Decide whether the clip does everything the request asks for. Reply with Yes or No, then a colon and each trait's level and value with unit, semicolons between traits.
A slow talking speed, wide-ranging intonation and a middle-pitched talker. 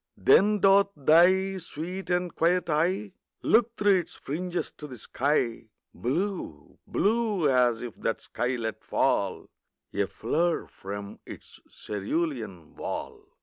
Yes: slow, 125 wpm; wide, 7.7 semitones; medium, 165 Hz